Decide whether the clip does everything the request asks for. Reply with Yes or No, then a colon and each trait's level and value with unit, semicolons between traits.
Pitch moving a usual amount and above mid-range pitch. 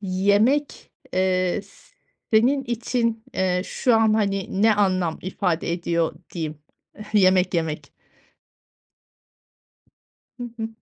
Yes: average, 3.6 semitones; high, 195 Hz